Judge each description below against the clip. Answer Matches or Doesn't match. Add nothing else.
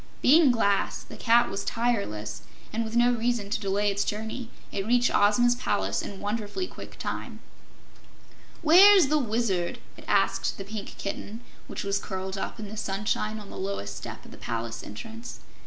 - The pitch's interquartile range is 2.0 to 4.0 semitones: Matches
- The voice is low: Doesn't match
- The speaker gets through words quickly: Doesn't match